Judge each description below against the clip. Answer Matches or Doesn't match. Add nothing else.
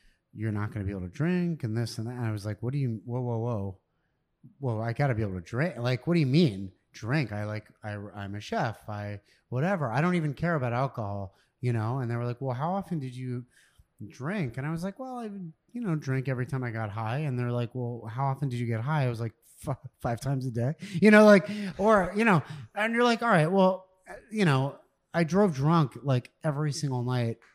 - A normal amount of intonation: Doesn't match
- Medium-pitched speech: Doesn't match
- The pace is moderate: Doesn't match